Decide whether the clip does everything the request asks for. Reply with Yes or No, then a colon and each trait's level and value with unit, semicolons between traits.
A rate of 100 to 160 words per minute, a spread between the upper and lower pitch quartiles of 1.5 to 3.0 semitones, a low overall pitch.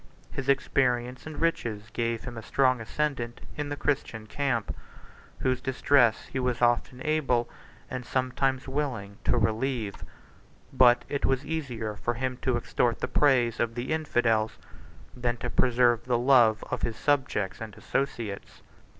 Yes: average, 150 wpm; narrow, 2.6 semitones; low, 125 Hz